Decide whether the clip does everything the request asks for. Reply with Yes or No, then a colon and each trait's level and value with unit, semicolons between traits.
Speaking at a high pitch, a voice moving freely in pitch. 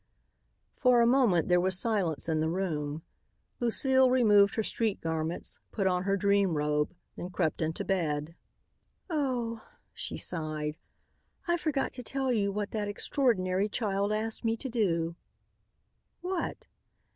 Yes: high, 200 Hz; wide, 5.9 semitones